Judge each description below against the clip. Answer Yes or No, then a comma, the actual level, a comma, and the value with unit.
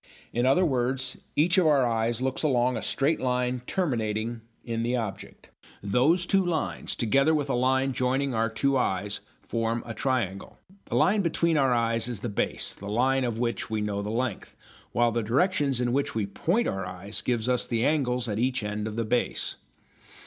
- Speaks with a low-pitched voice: Yes, low, 125 Hz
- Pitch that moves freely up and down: No, average, 3.2 semitones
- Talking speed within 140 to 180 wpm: No, average, 190 wpm